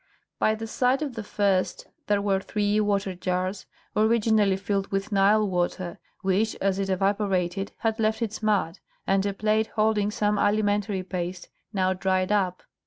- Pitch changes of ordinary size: No, narrow, 2.1 semitones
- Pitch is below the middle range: No, high, 200 Hz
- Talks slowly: No, average, 160 wpm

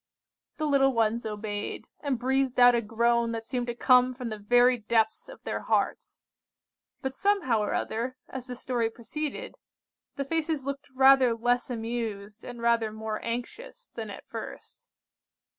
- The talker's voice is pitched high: Yes, high, 245 Hz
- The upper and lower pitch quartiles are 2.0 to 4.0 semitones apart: Yes, average, 2.8 semitones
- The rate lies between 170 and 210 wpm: No, average, 160 wpm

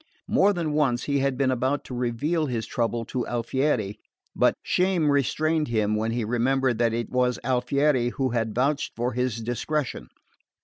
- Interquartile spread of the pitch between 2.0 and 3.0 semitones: No, average, 3.4 semitones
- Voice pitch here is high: No, low, 125 Hz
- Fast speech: No, average, 170 wpm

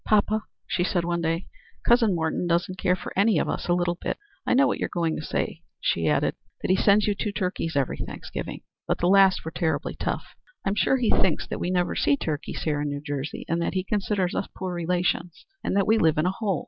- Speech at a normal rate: No, fast, 235 wpm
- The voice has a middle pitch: Yes, medium, 180 Hz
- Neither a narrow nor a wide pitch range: Yes, average, 3.3 semitones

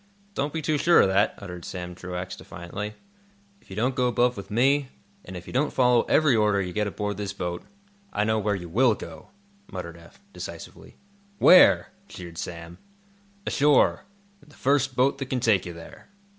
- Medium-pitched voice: No, low, 105 Hz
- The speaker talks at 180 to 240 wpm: Yes, average, 185 wpm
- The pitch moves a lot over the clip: Yes, wide, 6.7 semitones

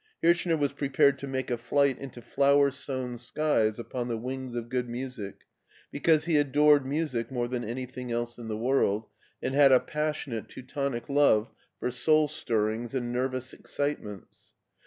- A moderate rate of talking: Yes, average, 165 wpm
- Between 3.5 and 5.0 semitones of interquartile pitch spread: No, average, 3.0 semitones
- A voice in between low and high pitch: No, low, 130 Hz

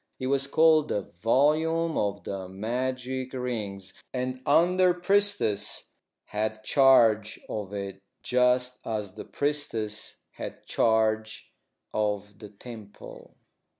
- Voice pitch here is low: Yes, low, 120 Hz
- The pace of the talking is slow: Yes, slow, 115 wpm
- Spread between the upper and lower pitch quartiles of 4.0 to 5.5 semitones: Yes, average, 4.7 semitones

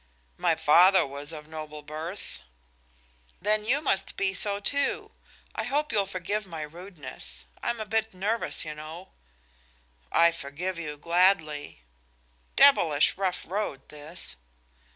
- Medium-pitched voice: Yes, medium, 175 Hz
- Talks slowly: Yes, slow, 130 wpm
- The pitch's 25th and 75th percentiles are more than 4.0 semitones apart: Yes, average, 4.8 semitones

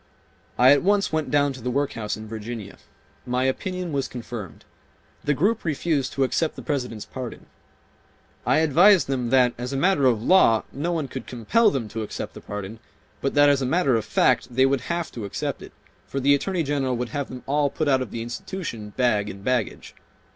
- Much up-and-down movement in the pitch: No, average, 3.9 semitones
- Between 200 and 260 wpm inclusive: Yes, fast, 205 wpm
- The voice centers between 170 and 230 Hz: No, low, 130 Hz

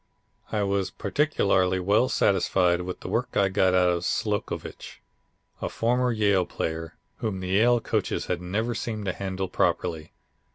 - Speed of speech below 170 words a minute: Yes, average, 155 wpm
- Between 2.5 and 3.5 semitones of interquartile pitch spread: Yes, average, 3.1 semitones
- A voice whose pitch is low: Yes, very low, 95 Hz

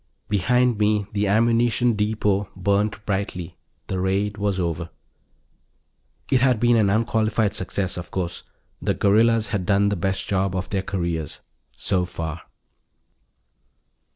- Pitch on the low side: Yes, low, 100 Hz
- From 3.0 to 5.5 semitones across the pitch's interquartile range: No, narrow, 2.6 semitones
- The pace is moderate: No, slow, 130 wpm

